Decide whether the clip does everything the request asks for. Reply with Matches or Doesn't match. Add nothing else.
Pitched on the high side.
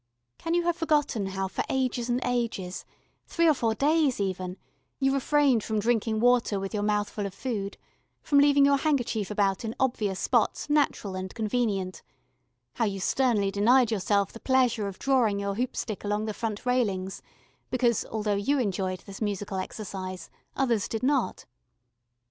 Matches